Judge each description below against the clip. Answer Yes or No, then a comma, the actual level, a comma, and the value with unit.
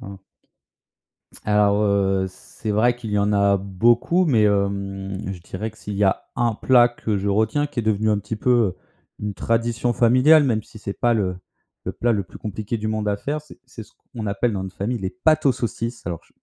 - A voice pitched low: Yes, low, 105 Hz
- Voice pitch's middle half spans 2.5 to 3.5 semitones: Yes, average, 3.1 semitones